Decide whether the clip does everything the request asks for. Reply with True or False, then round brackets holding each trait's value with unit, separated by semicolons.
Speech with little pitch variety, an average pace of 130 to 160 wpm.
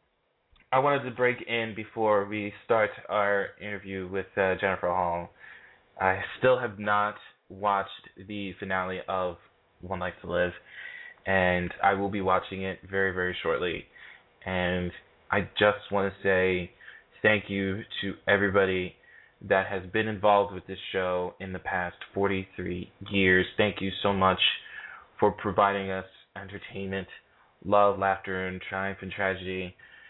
True (1.6 semitones; 140 wpm)